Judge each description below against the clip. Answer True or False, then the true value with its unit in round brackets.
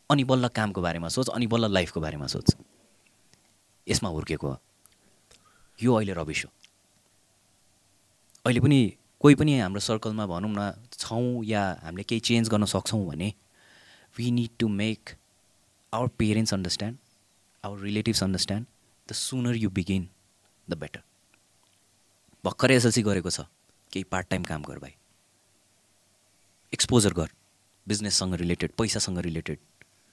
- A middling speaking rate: False (130 wpm)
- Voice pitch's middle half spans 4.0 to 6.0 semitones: False (3.0 semitones)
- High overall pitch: False (100 Hz)